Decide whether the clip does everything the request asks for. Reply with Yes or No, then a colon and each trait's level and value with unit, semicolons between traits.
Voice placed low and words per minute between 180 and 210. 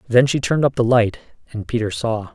No: low, 120 Hz; fast, 230 wpm